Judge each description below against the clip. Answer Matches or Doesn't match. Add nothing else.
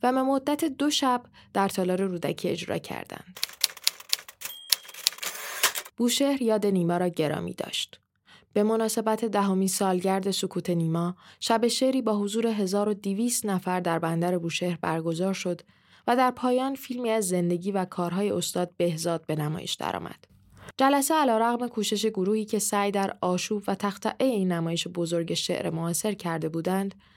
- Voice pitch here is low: Doesn't match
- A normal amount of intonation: Matches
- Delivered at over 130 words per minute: Matches